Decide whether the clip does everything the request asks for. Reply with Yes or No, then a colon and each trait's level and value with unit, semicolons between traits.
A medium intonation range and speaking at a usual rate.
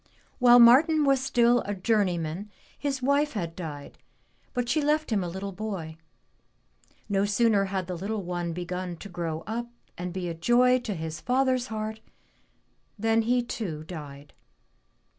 No: wide, 5.7 semitones; average, 155 wpm